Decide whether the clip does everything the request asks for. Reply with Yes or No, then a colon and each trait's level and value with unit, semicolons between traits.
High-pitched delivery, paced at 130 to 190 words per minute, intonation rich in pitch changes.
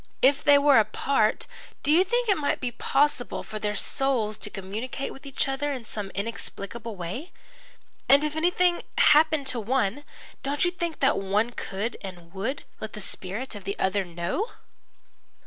Yes: high, 245 Hz; average, 175 wpm; wide, 5.9 semitones